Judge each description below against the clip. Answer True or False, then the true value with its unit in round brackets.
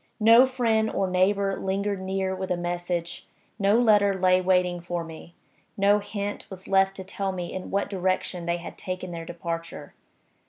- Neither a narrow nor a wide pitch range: False (2.2 semitones)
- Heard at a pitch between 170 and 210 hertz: True (190 Hz)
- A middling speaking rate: True (170 wpm)